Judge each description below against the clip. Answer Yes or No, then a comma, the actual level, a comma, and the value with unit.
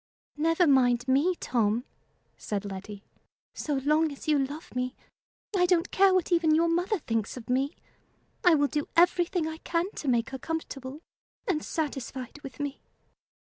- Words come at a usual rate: Yes, average, 160 wpm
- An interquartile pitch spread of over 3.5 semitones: Yes, average, 4.7 semitones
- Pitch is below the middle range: No, very high, 295 Hz